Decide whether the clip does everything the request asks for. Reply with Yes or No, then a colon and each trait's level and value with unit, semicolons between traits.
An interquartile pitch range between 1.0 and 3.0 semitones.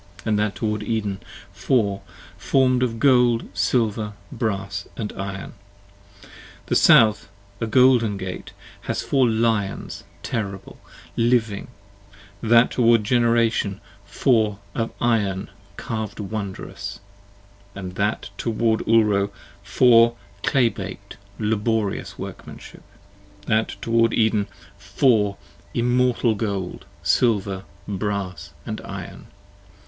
Yes: narrow, 2.6 semitones